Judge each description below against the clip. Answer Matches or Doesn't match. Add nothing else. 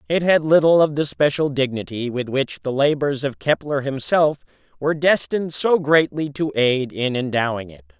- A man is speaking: Matches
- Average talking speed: Matches